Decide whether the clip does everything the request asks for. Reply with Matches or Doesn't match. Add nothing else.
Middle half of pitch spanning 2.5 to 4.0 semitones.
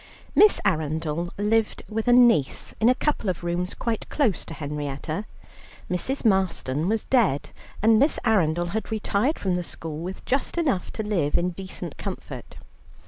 Doesn't match